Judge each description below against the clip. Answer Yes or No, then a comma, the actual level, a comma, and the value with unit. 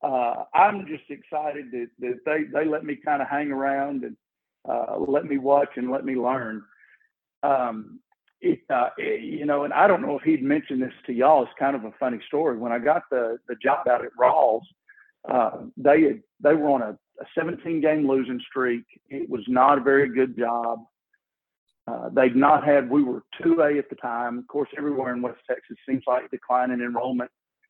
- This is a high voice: No, medium, 140 Hz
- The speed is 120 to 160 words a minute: No, average, 200 wpm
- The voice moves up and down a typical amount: Yes, average, 3.3 semitones